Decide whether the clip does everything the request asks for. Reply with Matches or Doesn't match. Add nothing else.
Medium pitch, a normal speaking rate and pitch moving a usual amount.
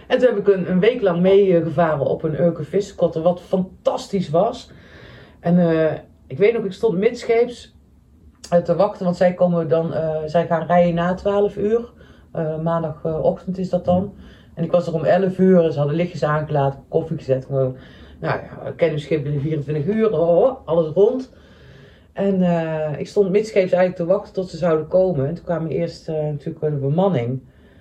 Matches